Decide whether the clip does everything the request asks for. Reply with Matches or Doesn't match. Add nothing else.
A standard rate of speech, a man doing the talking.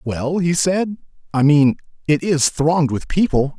Matches